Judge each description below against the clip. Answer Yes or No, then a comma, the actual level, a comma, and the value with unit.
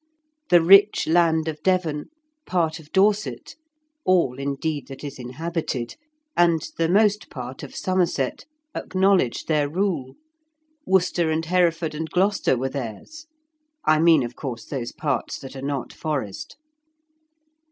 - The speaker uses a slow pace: Yes, slow, 130 wpm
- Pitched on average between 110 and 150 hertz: No, medium, 160 Hz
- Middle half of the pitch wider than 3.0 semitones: Yes, average, 4.7 semitones